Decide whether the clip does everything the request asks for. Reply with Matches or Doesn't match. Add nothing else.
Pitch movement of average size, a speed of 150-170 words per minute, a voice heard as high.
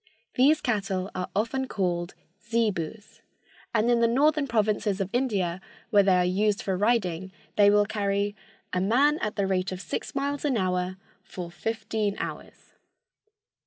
Matches